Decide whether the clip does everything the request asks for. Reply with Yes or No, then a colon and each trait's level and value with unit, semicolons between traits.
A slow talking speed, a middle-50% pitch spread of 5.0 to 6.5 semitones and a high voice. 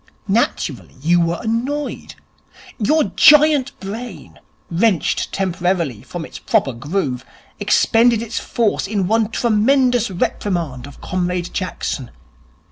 Yes: slow, 110 wpm; wide, 5.5 semitones; high, 195 Hz